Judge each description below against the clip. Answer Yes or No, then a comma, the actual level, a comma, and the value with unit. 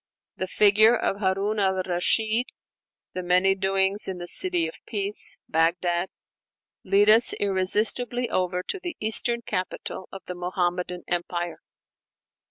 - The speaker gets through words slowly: Yes, slow, 130 wpm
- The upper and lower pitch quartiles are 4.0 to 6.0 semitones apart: No, average, 3.2 semitones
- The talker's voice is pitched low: No, high, 190 Hz